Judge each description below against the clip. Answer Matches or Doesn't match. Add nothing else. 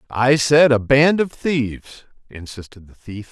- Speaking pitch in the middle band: Doesn't match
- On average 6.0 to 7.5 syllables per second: Doesn't match